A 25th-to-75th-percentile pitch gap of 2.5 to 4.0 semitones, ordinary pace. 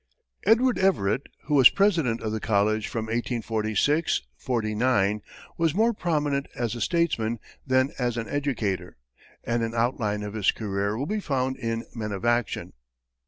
No: average, 4.9 semitones; average, 155 wpm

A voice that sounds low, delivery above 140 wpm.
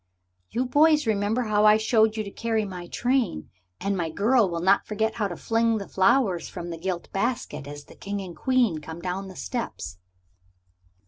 No: high, 205 Hz; average, 190 wpm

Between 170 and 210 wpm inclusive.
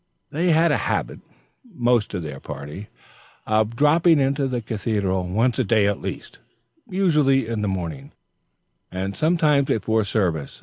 No: average, 145 wpm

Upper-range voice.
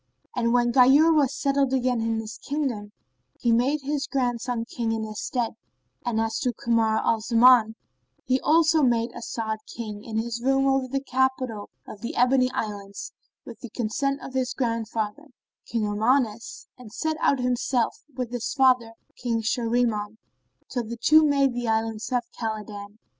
Yes: high, 240 Hz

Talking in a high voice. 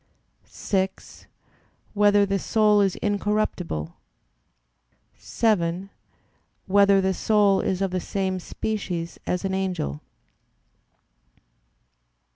Yes: high, 195 Hz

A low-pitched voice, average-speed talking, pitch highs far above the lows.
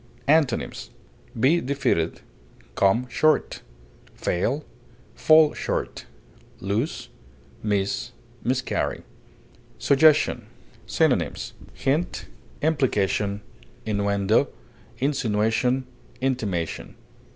No: low, 125 Hz; slow, 60 wpm; wide, 5.9 semitones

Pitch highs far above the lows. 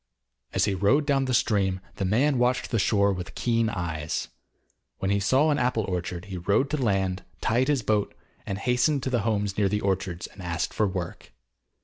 No: average, 4.7 semitones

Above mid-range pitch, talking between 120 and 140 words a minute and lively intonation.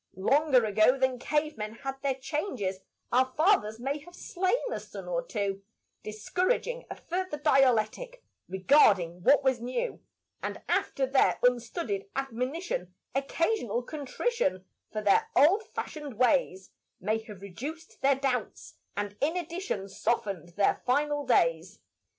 Yes: very high, 260 Hz; slow, 135 wpm; wide, 6.3 semitones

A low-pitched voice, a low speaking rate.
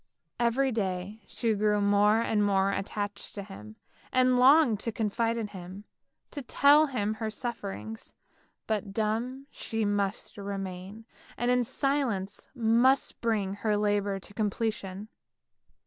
No: high, 215 Hz; slow, 130 wpm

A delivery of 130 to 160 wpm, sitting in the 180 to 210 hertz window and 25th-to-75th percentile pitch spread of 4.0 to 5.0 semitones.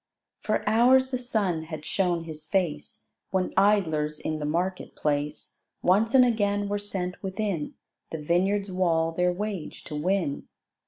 Yes: average, 150 wpm; medium, 185 Hz; average, 4.3 semitones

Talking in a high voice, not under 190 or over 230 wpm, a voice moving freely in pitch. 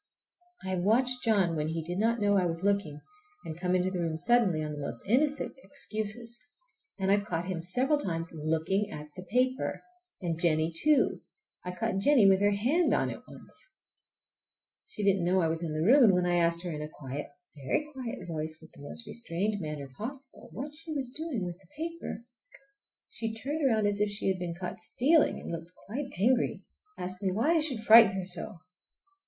Yes: high, 195 Hz; fast, 205 wpm; wide, 6.1 semitones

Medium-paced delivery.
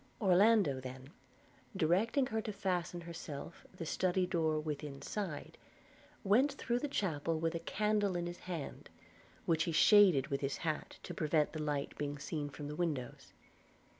Yes: average, 160 wpm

